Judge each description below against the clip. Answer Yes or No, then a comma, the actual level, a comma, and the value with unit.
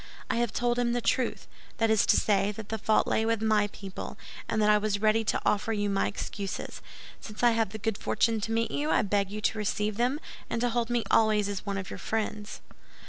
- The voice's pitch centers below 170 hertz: No, high, 215 Hz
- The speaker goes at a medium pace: No, fast, 240 wpm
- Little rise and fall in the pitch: Yes, narrow, 1.8 semitones